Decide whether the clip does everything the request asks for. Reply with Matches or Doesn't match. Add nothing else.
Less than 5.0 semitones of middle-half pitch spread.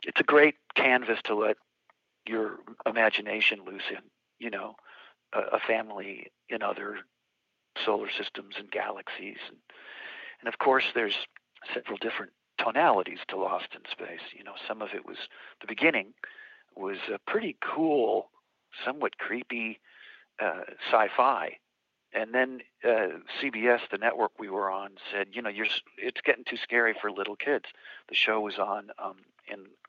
Matches